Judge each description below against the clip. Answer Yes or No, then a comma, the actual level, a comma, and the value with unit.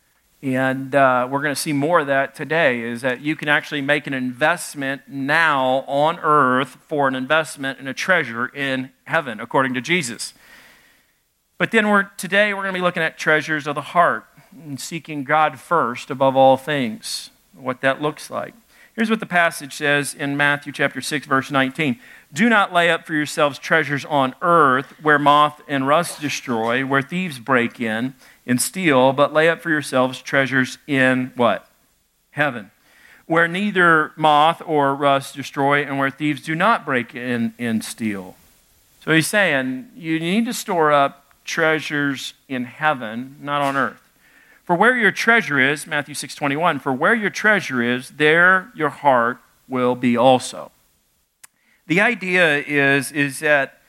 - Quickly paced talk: No, average, 165 wpm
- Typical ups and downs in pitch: Yes, average, 3.6 semitones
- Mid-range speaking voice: Yes, medium, 145 Hz